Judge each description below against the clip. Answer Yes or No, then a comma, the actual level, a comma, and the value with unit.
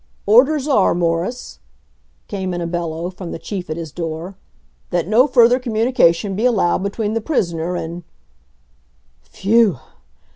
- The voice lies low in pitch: No, medium, 185 Hz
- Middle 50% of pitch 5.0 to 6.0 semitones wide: Yes, average, 5.3 semitones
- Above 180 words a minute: No, average, 145 wpm